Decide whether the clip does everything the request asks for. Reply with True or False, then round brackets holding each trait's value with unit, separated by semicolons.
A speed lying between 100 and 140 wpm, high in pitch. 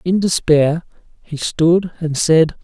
False (135 wpm; 165 Hz)